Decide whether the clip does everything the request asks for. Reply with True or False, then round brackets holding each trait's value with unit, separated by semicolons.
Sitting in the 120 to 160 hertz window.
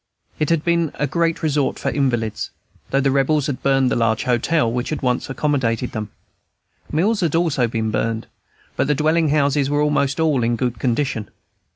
True (140 Hz)